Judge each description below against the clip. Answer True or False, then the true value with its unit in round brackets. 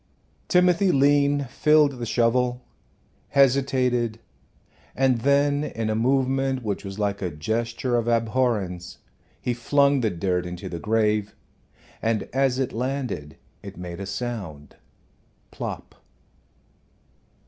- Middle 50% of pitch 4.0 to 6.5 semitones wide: True (4.4 semitones)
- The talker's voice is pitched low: True (120 Hz)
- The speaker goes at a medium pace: False (115 wpm)